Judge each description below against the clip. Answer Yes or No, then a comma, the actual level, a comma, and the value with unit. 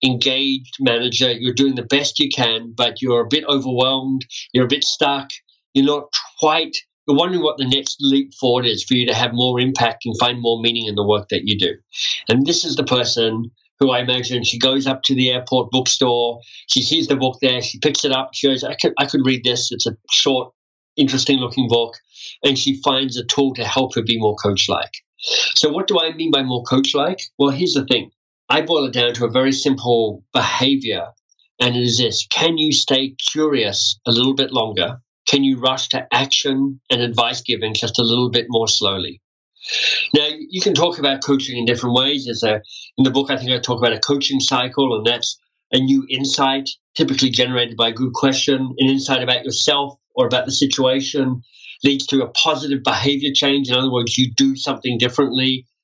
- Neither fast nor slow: No, fast, 210 wpm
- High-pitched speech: No, low, 130 Hz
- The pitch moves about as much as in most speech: No, narrow, 2.3 semitones